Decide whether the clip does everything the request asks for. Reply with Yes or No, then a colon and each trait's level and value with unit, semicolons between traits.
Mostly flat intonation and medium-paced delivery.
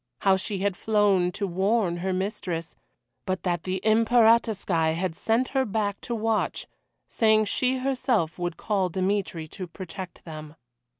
No: average, 3.7 semitones; average, 145 wpm